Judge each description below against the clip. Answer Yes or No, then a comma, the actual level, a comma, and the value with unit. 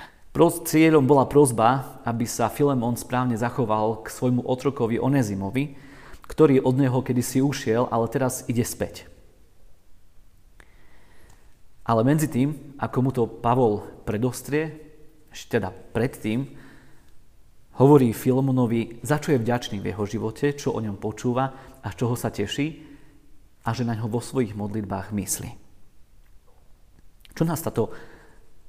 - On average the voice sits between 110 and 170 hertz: Yes, low, 120 Hz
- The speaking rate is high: No, average, 125 wpm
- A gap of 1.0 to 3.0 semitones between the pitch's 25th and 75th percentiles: No, average, 4.2 semitones